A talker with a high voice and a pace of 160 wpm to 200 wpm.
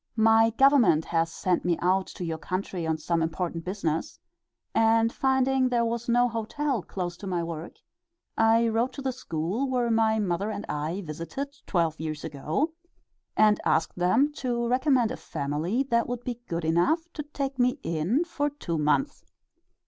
Yes: high, 220 Hz; average, 170 wpm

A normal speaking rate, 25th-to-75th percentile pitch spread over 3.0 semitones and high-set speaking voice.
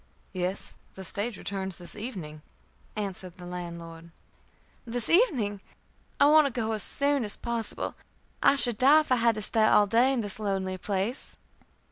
Yes: average, 165 wpm; average, 4.5 semitones; high, 210 Hz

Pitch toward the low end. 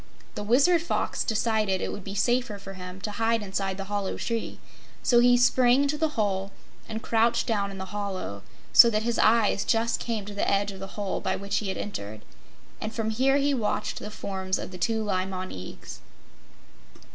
No: high, 210 Hz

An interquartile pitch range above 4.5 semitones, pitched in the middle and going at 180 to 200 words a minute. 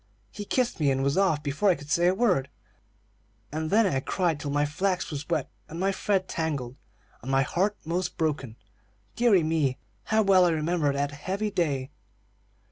Yes: average, 4.9 semitones; medium, 160 Hz; average, 185 wpm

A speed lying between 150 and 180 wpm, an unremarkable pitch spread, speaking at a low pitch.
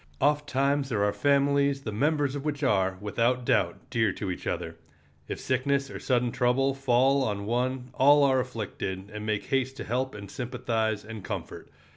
Yes: average, 175 wpm; average, 4.2 semitones; low, 125 Hz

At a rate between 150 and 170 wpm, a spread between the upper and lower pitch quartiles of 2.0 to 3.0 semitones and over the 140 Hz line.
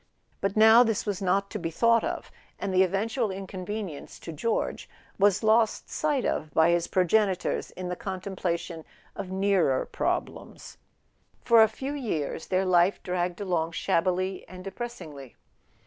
No: average, 155 wpm; average, 3.5 semitones; high, 190 Hz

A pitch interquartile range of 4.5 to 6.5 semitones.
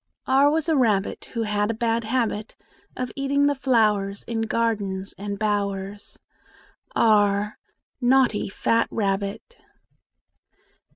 No: average, 3.7 semitones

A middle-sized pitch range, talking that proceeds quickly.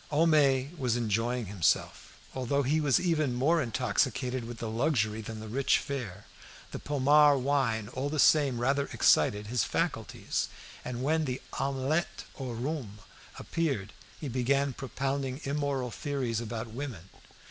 No: average, 3.5 semitones; average, 140 wpm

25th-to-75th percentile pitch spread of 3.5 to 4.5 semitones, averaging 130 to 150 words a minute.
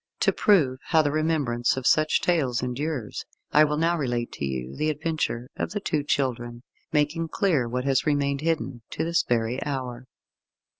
No: average, 4.1 semitones; average, 170 wpm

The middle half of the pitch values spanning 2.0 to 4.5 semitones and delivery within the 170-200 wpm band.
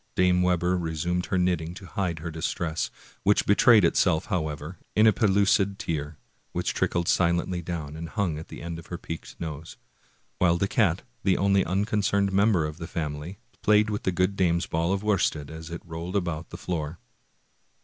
Yes: average, 3.1 semitones; average, 180 wpm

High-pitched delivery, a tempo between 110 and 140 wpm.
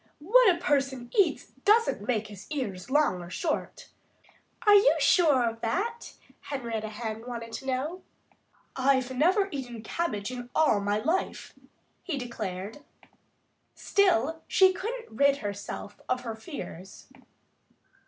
Yes: very high, 260 Hz; slow, 135 wpm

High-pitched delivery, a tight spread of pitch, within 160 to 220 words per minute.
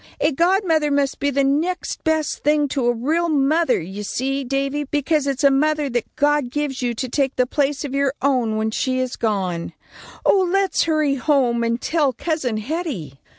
No: very high, 275 Hz; average, 3.5 semitones; average, 190 wpm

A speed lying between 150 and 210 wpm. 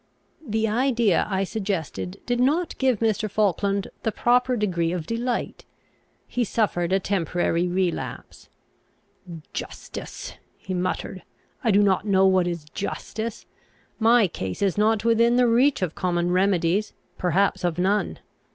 No: slow, 135 wpm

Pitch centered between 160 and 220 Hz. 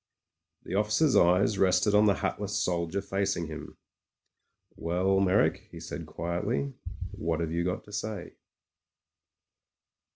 No: very low, 95 Hz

